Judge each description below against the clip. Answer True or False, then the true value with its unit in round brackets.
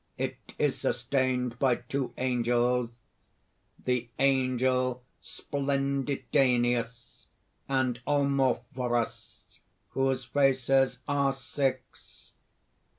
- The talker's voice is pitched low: True (130 Hz)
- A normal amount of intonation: False (1.8 semitones)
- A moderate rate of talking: False (70 wpm)